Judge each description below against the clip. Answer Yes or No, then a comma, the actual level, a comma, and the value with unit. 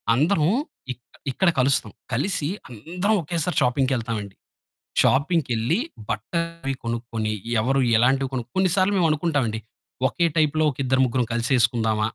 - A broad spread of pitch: Yes, wide, 5.9 semitones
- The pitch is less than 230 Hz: Yes, low, 135 Hz